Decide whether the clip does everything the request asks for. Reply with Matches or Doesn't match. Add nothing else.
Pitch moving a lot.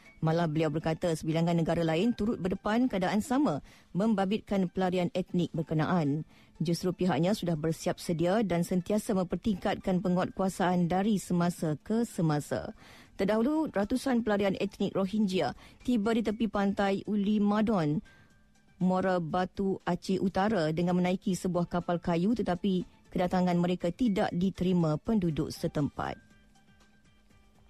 Doesn't match